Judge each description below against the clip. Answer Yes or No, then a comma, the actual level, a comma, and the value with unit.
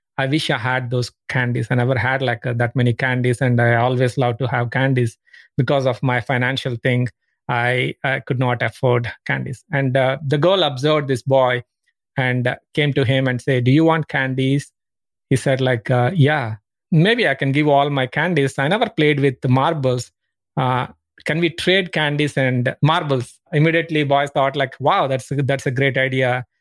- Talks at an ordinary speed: Yes, average, 190 wpm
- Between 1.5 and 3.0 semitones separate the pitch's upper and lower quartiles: Yes, narrow, 2.5 semitones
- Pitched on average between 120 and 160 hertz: Yes, low, 135 Hz